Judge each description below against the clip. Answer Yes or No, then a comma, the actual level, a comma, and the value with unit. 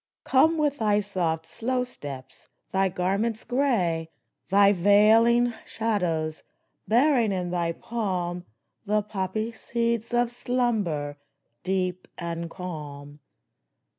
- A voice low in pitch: No, high, 200 Hz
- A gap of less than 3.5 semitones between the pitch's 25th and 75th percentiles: No, average, 5.2 semitones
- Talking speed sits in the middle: No, slow, 105 wpm